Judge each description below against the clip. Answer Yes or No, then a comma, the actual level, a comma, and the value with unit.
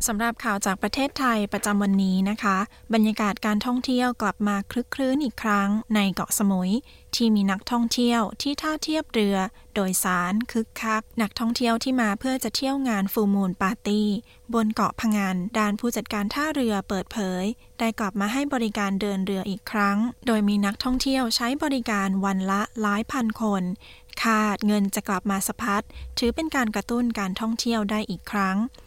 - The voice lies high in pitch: Yes, high, 215 Hz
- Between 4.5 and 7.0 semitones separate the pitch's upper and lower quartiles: No, average, 2.9 semitones